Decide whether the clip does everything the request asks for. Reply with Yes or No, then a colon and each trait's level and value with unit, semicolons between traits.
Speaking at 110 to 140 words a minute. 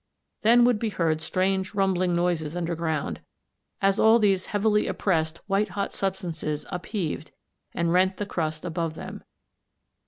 Yes: slow, 135 wpm